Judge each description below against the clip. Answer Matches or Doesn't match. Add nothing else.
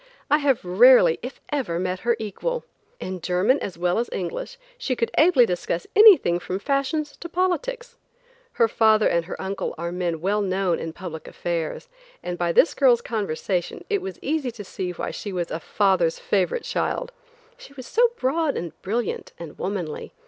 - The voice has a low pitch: Doesn't match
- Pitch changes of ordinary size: Doesn't match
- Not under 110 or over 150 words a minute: Doesn't match